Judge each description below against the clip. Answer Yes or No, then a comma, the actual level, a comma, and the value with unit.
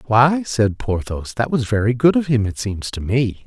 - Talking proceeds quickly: Yes, fast, 225 wpm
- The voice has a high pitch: No, low, 120 Hz